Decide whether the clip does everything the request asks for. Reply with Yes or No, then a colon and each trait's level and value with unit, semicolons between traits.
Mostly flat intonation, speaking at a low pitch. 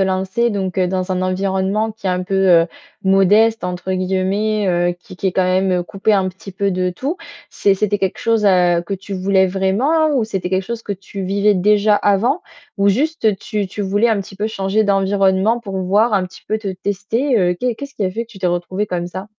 No: narrow, 2.3 semitones; high, 195 Hz